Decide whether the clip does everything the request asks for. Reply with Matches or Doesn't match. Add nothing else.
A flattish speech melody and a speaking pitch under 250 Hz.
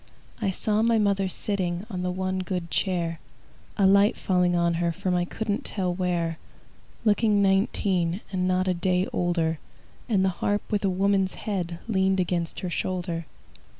Matches